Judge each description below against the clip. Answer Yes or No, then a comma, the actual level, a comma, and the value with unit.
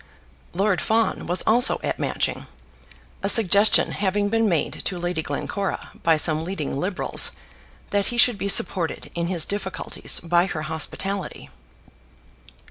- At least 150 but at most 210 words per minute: No, slow, 135 wpm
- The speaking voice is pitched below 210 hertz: Yes, high, 190 Hz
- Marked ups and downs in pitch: No, average, 3.2 semitones